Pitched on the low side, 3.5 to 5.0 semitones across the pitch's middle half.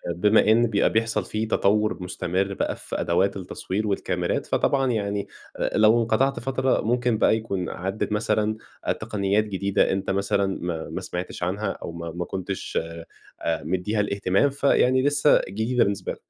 No: low, 105 Hz; average, 2.8 semitones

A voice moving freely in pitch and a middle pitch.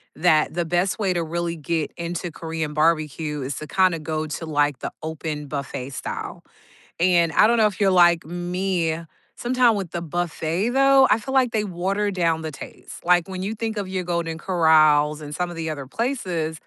No: average, 3.3 semitones; medium, 170 Hz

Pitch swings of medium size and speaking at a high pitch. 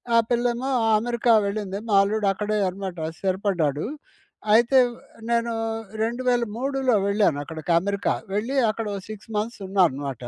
Yes: average, 3.7 semitones; high, 210 Hz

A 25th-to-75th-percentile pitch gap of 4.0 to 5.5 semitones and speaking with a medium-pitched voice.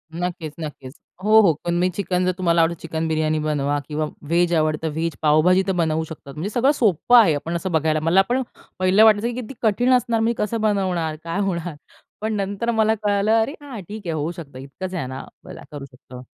Yes: average, 5.0 semitones; medium, 175 Hz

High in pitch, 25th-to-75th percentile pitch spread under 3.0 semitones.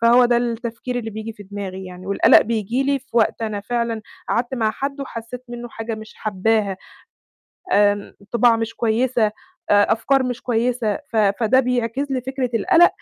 Yes: high, 230 Hz; narrow, 2.5 semitones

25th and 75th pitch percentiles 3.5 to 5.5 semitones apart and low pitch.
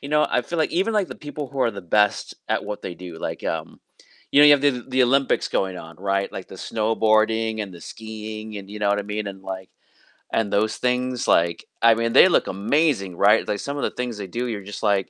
Yes: average, 4.3 semitones; low, 110 Hz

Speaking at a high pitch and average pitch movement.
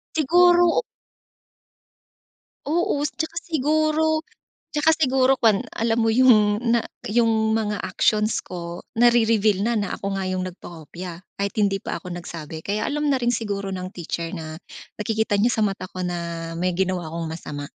No: high, 210 Hz; wide, 5.8 semitones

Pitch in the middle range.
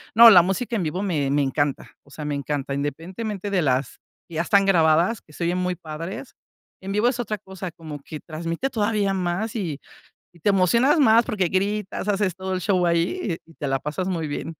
Yes: medium, 180 Hz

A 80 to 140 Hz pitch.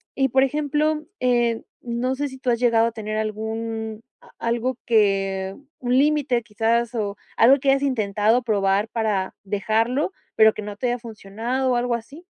No: high, 230 Hz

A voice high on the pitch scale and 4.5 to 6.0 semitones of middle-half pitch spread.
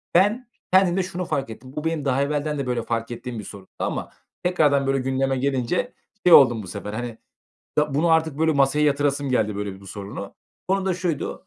No: medium, 140 Hz; average, 5.1 semitones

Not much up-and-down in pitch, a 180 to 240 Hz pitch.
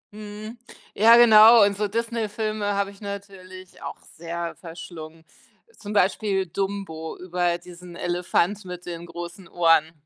No: average, 3.3 semitones; high, 190 Hz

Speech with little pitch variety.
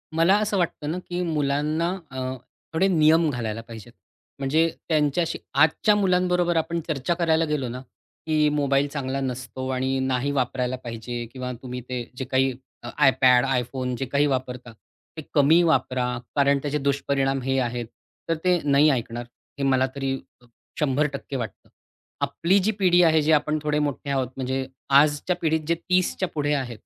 No: average, 3.7 semitones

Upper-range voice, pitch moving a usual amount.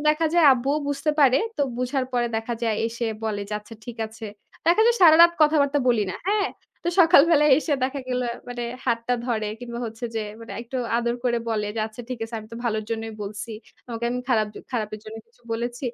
Yes: high, 240 Hz; average, 3.9 semitones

